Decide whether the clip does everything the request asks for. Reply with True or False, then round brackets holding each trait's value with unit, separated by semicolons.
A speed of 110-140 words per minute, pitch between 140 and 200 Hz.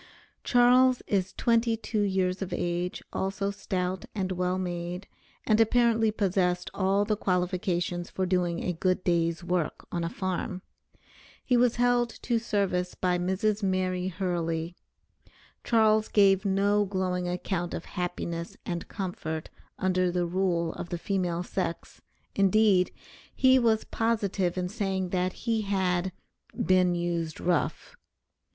True (135 wpm; 185 Hz)